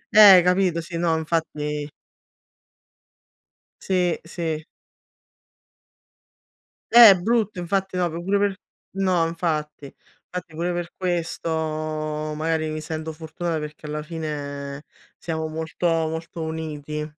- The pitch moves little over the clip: Yes, narrow, 2.3 semitones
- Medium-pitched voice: Yes, medium, 160 Hz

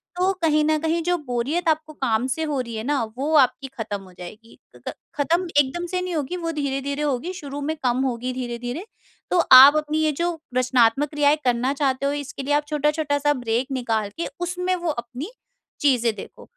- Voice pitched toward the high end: Yes, very high, 285 Hz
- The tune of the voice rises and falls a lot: No, average, 3.9 semitones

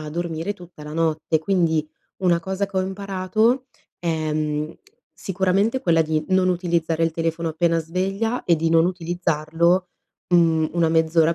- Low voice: No, medium, 170 Hz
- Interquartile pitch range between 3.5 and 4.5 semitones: No, narrow, 2.5 semitones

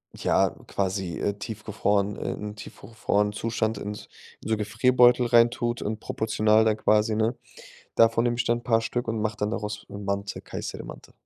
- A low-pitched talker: Yes, low, 110 Hz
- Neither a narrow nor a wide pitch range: No, narrow, 1.8 semitones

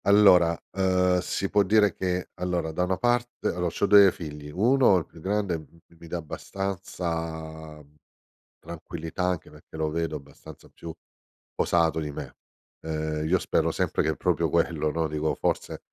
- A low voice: Yes, very low, 85 Hz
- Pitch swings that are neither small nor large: Yes, average, 3.2 semitones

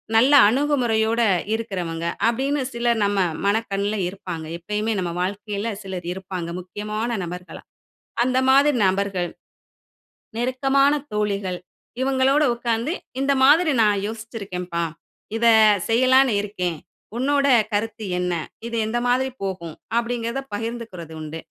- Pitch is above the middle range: Yes, high, 220 Hz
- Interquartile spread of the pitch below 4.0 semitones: No, average, 5.0 semitones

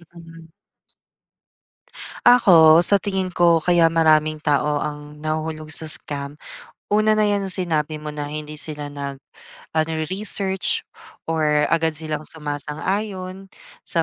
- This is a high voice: No, medium, 160 Hz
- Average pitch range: Yes, average, 3.4 semitones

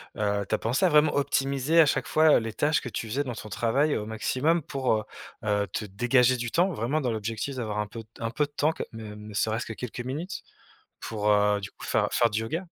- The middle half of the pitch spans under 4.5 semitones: No, average, 4.9 semitones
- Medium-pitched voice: No, low, 120 Hz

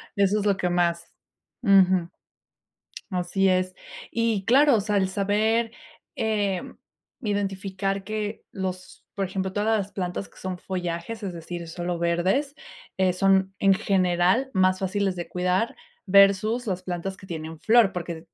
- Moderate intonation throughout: No, narrow, 2.3 semitones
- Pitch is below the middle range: No, high, 190 Hz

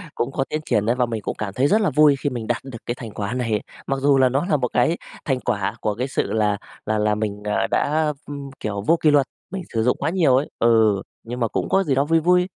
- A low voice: Yes, low, 130 Hz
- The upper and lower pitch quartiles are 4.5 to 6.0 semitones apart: Yes, average, 5.1 semitones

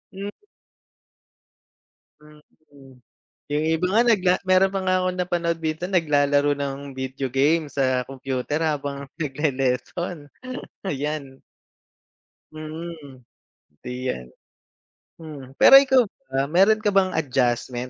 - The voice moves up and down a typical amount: Yes, average, 4.3 semitones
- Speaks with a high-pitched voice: No, medium, 150 Hz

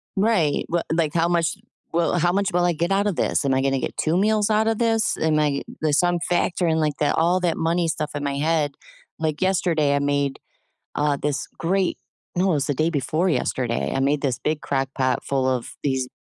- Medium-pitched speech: Yes, medium, 160 Hz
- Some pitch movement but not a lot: Yes, average, 3.7 semitones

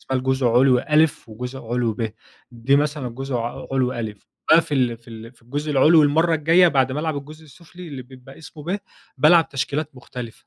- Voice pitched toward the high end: No, low, 135 Hz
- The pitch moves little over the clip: No, average, 3.7 semitones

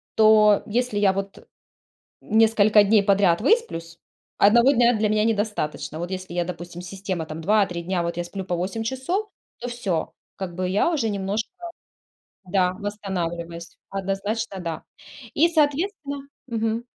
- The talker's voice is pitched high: Yes, high, 205 Hz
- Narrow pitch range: No, average, 3.8 semitones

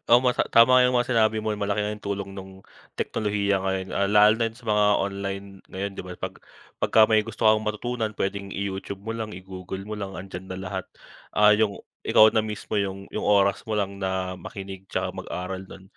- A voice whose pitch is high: No, low, 100 Hz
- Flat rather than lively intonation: Yes, narrow, 2.1 semitones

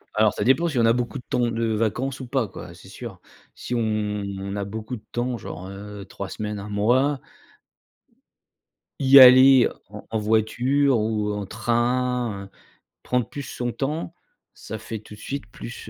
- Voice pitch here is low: Yes, low, 115 Hz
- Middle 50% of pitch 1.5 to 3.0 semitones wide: No, average, 3.4 semitones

